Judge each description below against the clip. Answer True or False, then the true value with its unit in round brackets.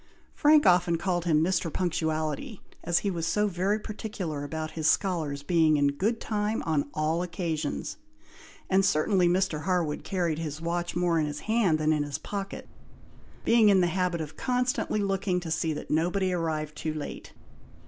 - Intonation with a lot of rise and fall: False (3.7 semitones)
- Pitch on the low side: False (175 Hz)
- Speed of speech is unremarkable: True (170 wpm)